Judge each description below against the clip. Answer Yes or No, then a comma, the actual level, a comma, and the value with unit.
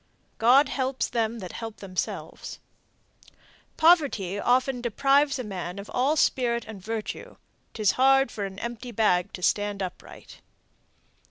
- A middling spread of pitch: Yes, average, 4.6 semitones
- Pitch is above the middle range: Yes, high, 230 Hz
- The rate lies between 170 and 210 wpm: No, slow, 135 wpm